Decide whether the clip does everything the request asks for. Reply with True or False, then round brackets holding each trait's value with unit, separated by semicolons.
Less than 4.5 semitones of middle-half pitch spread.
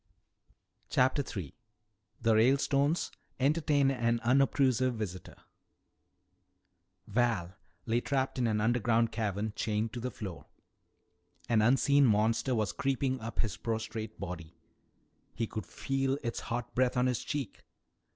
True (3.3 semitones)